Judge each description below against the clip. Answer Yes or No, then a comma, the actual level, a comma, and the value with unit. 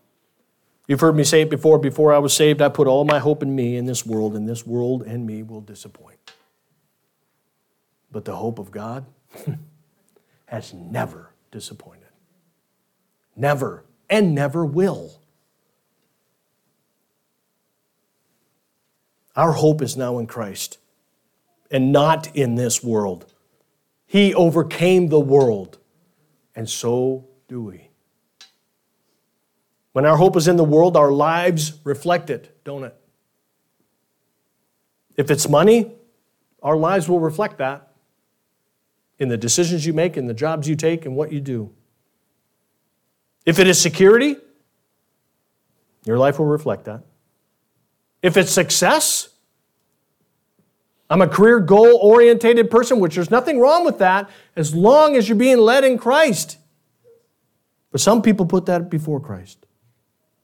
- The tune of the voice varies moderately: No, wide, 6.0 semitones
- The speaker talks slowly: Yes, slow, 130 wpm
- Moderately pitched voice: Yes, medium, 155 Hz